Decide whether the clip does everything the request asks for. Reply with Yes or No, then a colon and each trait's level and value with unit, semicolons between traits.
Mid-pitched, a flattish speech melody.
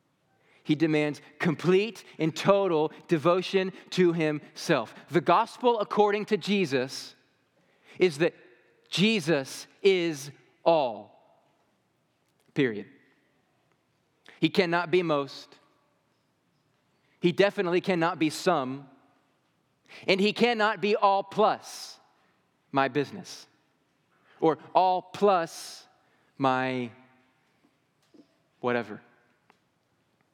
No: medium, 165 Hz; wide, 5.4 semitones